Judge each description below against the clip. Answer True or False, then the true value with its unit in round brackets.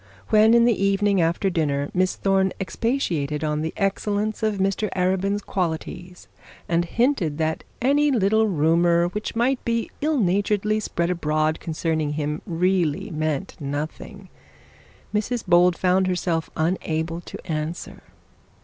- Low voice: False (180 Hz)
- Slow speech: True (130 wpm)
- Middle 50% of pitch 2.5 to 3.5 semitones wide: False (4.4 semitones)